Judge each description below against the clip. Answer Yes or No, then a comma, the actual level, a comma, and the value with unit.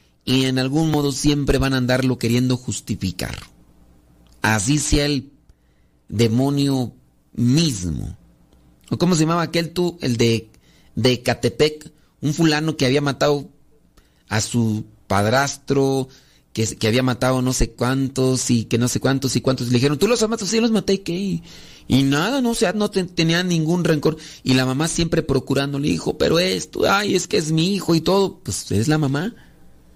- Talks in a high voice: No, low, 130 Hz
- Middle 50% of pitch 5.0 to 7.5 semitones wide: Yes, average, 5.3 semitones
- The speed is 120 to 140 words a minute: No, average, 175 wpm